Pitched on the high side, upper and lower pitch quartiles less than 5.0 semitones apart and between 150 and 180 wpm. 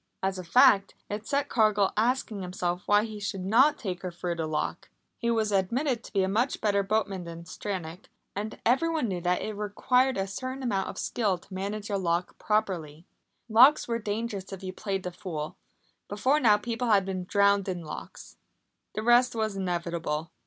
No: high, 200 Hz; average, 3.6 semitones; average, 190 wpm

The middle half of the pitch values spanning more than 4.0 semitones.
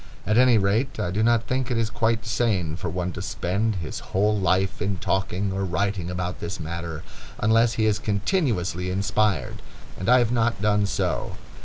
No: average, 3.7 semitones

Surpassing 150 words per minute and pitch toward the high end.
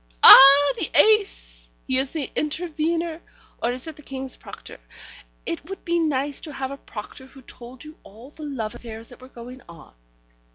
Yes: average, 180 wpm; very high, 270 Hz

